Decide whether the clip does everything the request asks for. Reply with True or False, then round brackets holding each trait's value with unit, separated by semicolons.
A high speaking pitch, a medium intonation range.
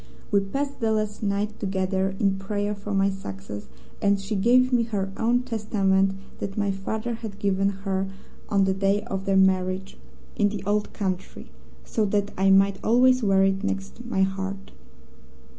False (200 Hz; 1.7 semitones)